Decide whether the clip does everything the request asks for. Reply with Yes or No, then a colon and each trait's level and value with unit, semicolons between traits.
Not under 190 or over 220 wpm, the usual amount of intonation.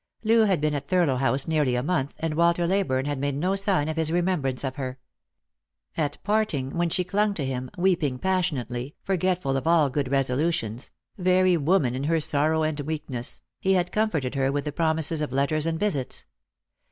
Yes: average, 195 wpm; average, 4.7 semitones